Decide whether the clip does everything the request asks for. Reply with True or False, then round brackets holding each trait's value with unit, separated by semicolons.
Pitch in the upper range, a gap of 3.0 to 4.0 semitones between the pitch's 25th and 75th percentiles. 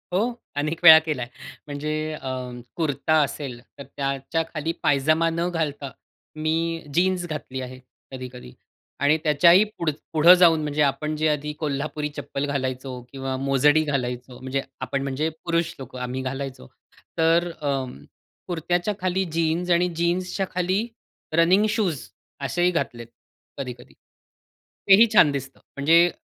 False (150 Hz; 3.7 semitones)